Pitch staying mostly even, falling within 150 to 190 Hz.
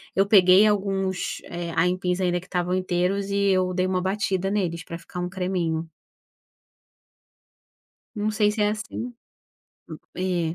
Yes: narrow, 1.7 semitones; medium, 185 Hz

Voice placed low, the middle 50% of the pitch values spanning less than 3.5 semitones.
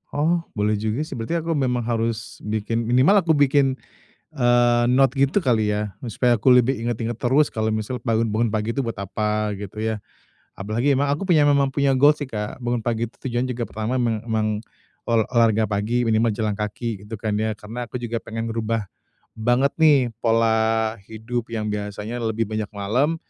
Yes: low, 115 Hz; average, 2.9 semitones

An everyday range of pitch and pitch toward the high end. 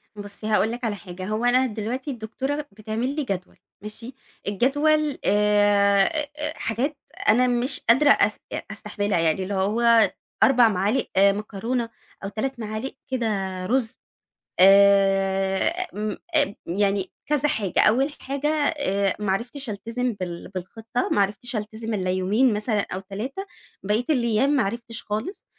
Yes: average, 4.2 semitones; high, 220 Hz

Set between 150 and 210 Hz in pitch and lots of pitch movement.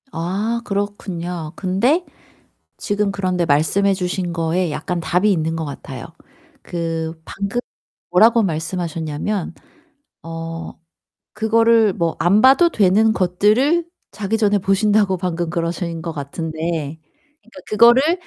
No: medium, 185 Hz; average, 4.2 semitones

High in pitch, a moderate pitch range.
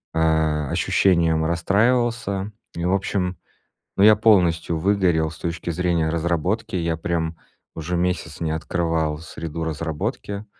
No: very low, 85 Hz; average, 3.0 semitones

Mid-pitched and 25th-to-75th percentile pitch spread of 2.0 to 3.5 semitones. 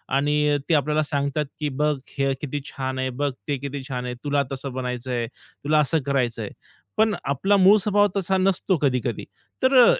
Yes: medium, 145 Hz; average, 2.8 semitones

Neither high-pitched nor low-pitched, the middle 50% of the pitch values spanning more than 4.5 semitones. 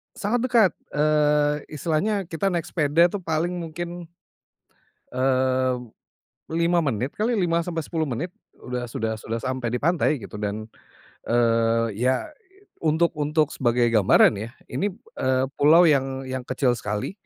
Yes: medium, 145 Hz; wide, 5.4 semitones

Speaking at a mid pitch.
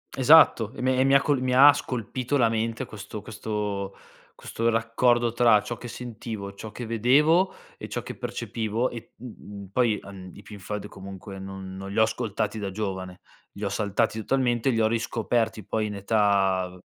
No: low, 110 Hz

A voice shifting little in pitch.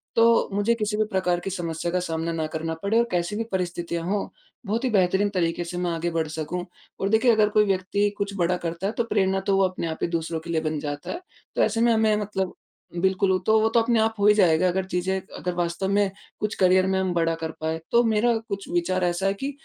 No: average, 3.5 semitones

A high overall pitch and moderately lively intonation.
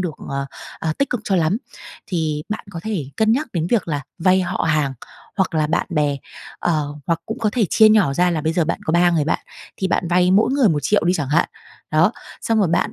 No: medium, 175 Hz; average, 4.8 semitones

